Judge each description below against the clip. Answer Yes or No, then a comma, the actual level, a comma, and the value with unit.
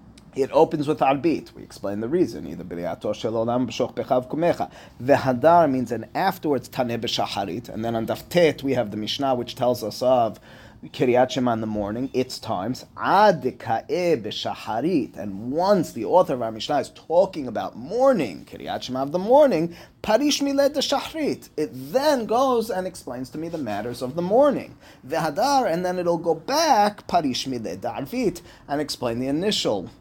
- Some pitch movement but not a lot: No, wide, 7.9 semitones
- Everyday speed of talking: Yes, average, 165 wpm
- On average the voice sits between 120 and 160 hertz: Yes, medium, 140 Hz